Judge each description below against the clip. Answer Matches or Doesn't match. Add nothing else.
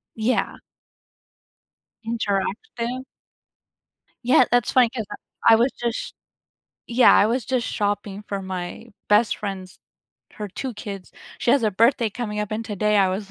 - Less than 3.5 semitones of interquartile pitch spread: Matches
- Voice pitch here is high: Matches